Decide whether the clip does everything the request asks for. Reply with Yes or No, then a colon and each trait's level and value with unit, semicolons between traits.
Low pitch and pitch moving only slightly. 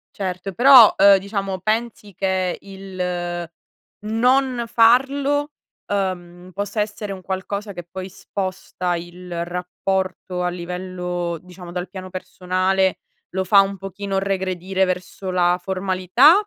No: high, 190 Hz; narrow, 1.9 semitones